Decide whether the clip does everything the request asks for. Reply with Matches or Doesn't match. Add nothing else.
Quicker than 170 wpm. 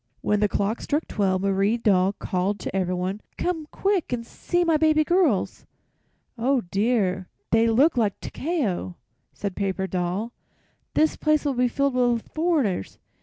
Doesn't match